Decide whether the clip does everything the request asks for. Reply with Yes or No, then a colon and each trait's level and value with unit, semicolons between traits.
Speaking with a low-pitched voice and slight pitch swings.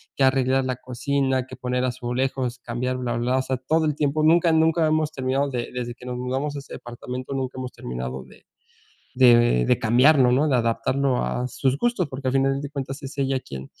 Yes: low, 130 Hz; narrow, 2.0 semitones